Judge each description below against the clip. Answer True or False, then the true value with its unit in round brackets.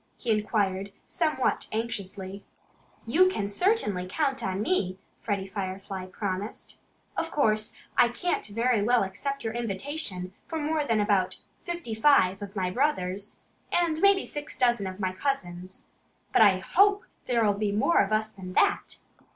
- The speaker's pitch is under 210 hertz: False (215 Hz)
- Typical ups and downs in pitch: False (6.4 semitones)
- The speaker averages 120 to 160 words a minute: True (150 wpm)